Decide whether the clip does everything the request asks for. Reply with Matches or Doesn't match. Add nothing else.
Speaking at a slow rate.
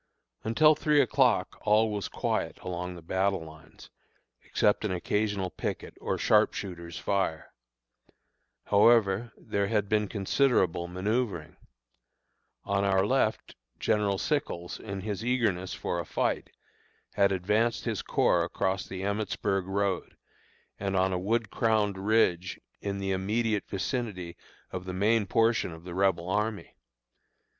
Matches